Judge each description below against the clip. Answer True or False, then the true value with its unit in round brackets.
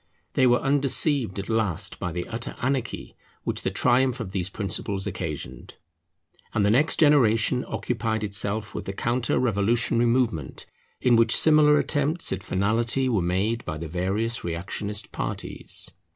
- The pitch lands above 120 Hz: False (110 Hz)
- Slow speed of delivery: False (150 wpm)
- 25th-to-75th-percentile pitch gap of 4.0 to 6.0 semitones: True (4.4 semitones)